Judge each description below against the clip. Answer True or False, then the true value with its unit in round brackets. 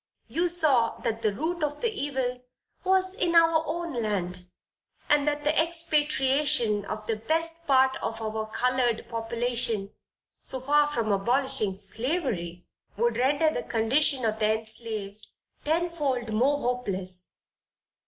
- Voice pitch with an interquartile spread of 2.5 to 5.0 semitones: False (5.5 semitones)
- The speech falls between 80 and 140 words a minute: True (135 wpm)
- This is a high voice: True (250 Hz)